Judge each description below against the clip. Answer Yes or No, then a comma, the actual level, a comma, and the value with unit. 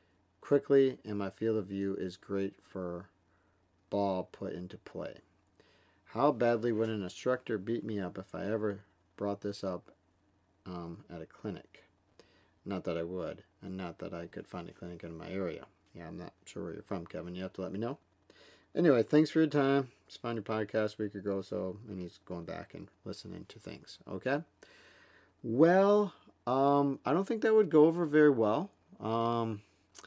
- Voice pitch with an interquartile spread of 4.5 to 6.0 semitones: Yes, average, 4.8 semitones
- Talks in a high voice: No, low, 100 Hz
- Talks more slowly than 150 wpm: No, average, 190 wpm